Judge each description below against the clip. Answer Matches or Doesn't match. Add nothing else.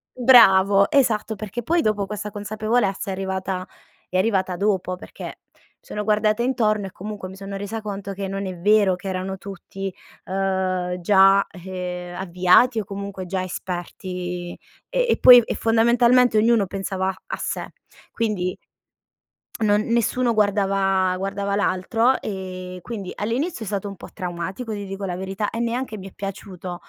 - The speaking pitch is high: Matches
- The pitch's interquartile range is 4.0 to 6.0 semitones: Doesn't match